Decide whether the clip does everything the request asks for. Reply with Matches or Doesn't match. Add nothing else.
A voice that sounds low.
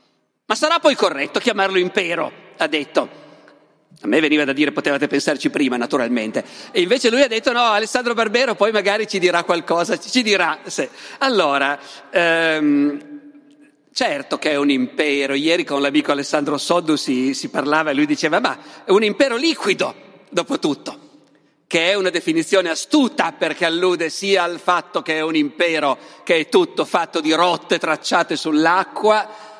Doesn't match